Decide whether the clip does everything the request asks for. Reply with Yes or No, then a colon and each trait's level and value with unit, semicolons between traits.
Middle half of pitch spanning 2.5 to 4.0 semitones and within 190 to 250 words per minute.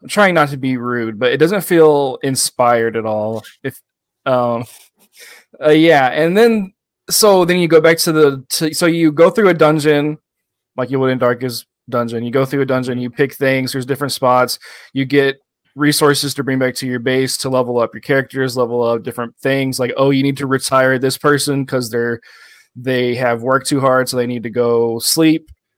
Yes: average, 3.4 semitones; fast, 205 wpm